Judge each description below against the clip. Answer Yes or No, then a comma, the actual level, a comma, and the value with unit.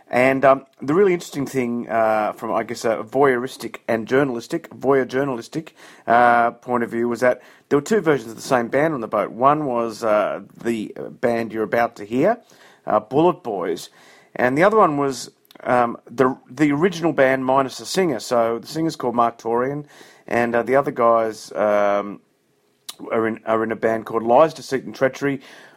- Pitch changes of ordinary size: Yes, average, 3.0 semitones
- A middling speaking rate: Yes, average, 190 wpm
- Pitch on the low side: Yes, low, 120 Hz